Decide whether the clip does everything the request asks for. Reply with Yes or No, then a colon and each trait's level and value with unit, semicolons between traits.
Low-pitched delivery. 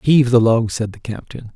Yes: low, 115 Hz